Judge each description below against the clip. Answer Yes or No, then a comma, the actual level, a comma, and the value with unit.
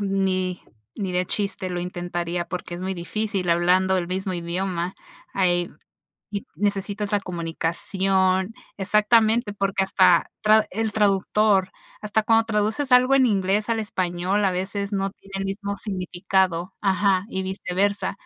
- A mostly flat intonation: Yes, narrow, 2.2 semitones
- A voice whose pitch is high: Yes, high, 195 Hz